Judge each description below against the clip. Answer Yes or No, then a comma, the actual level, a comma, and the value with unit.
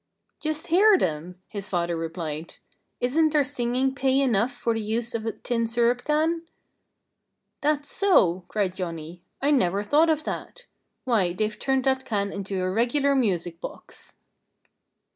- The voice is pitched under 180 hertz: No, high, 235 Hz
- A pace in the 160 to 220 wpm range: No, average, 150 wpm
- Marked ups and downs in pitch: Yes, wide, 7.1 semitones